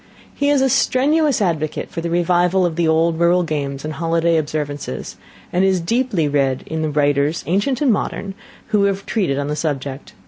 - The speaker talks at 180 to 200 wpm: Yes, average, 185 wpm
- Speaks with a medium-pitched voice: Yes, medium, 165 Hz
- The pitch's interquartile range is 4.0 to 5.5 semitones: Yes, average, 4.6 semitones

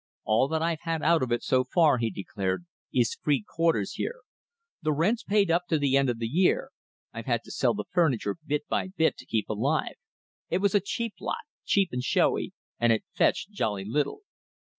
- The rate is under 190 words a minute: No, fast, 205 wpm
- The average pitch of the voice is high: No, medium, 150 Hz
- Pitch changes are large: Yes, wide, 6.8 semitones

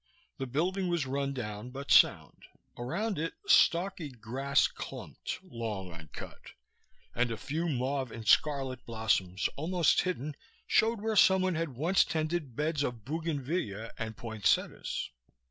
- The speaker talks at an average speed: No, slow, 130 wpm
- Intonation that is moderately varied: No, wide, 6.2 semitones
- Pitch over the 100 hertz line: Yes, medium, 140 Hz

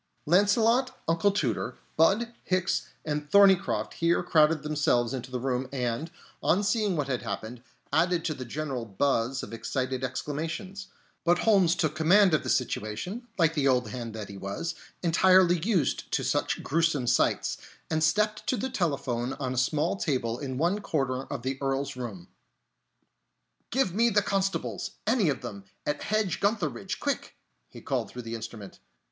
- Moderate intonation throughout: No, wide, 6.6 semitones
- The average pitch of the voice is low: No, medium, 150 Hz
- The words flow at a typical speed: Yes, average, 165 wpm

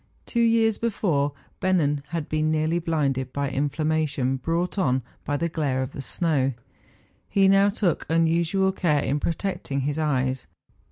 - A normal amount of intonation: Yes, average, 4.1 semitones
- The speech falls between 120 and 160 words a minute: Yes, average, 155 wpm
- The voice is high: No, medium, 155 Hz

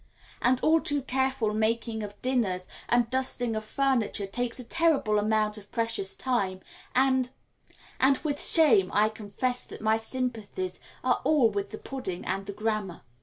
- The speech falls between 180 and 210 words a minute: No, average, 160 wpm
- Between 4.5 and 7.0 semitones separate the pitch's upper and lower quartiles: No, average, 3.7 semitones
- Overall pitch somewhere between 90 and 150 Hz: No, high, 230 Hz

